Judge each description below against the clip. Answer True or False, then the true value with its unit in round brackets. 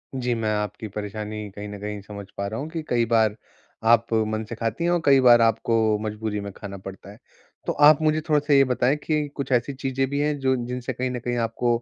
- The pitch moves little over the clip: False (4.0 semitones)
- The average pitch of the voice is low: True (115 Hz)